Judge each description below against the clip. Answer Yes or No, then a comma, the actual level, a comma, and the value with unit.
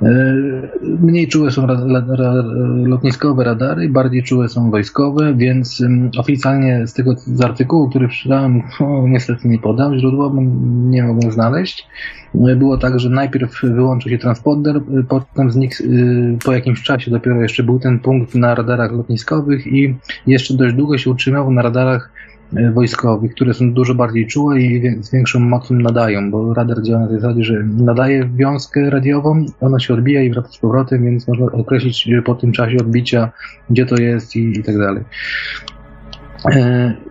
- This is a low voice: Yes, low, 125 Hz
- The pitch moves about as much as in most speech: No, narrow, 1.8 semitones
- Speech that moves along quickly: Yes, fast, 165 wpm